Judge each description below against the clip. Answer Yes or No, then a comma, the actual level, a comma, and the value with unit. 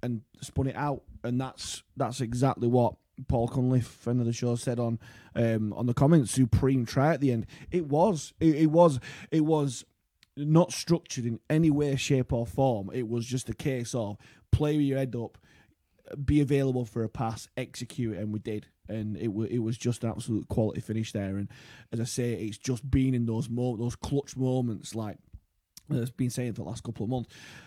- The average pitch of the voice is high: No, low, 120 Hz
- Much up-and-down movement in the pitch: No, average, 3.0 semitones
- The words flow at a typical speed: No, fast, 210 wpm